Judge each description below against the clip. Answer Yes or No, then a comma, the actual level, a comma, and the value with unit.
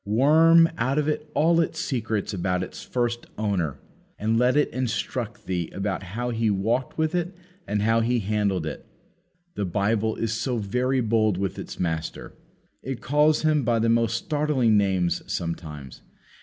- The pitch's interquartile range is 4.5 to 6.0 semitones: Yes, average, 4.8 semitones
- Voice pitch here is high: No, low, 115 Hz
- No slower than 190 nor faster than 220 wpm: No, average, 160 wpm